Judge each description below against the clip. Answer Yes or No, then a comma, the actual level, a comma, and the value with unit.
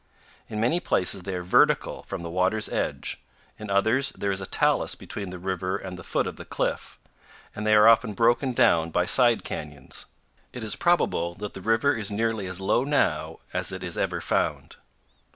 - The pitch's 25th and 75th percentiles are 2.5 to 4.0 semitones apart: Yes, average, 3.7 semitones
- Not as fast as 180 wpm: No, average, 195 wpm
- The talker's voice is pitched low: Yes, low, 100 Hz